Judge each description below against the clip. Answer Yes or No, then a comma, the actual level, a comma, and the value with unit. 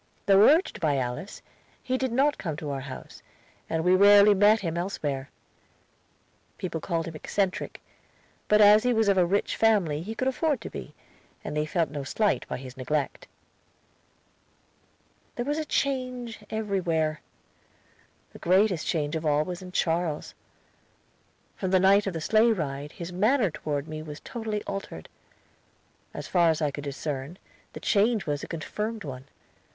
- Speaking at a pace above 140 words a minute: Yes, average, 165 wpm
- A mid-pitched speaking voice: Yes, medium, 180 Hz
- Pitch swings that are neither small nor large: No, wide, 5.8 semitones